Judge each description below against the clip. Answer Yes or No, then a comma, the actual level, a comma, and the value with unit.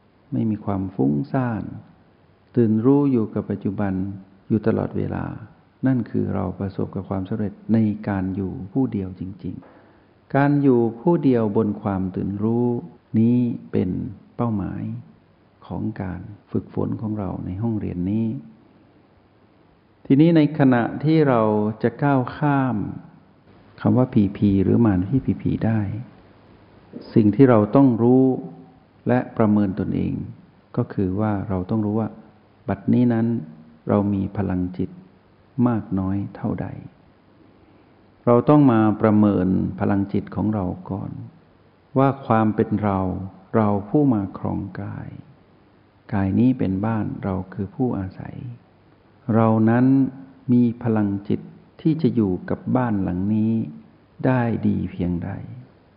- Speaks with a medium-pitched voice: No, low, 105 Hz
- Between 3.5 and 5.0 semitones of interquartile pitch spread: Yes, average, 3.8 semitones